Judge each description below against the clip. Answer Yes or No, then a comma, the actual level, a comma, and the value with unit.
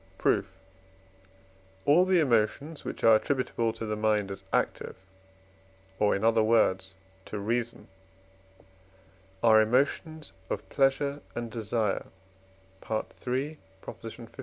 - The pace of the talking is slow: Yes, slow, 105 wpm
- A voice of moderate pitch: No, low, 115 Hz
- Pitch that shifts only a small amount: No, average, 4.5 semitones